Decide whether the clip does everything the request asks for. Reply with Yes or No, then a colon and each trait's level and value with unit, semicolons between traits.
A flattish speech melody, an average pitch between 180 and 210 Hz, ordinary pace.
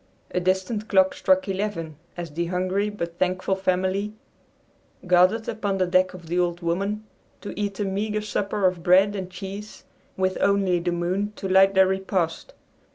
Yes: narrow, 2.0 semitones; high, 190 Hz; average, 165 wpm